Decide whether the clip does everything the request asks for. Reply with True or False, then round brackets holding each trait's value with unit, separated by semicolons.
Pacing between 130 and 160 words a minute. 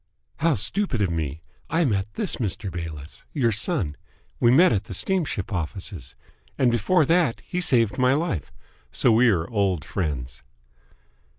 True (155 wpm)